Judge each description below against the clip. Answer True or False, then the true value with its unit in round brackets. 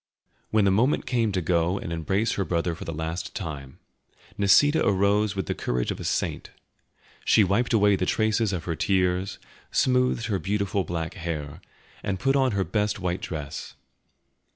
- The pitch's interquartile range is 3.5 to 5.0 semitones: True (4.0 semitones)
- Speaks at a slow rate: False (175 wpm)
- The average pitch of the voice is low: True (95 Hz)